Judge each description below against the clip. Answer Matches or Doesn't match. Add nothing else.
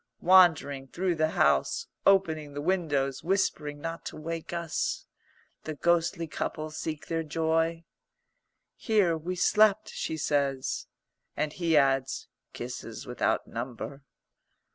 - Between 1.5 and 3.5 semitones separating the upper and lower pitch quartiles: Matches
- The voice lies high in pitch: Doesn't match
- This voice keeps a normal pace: Doesn't match